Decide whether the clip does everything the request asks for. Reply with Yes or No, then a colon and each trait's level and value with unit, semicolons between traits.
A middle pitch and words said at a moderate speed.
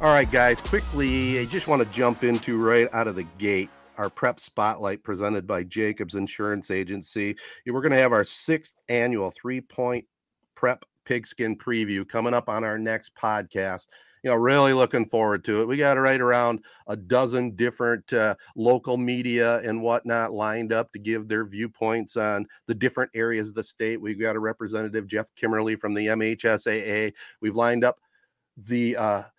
No: low, 115 Hz; average, 180 wpm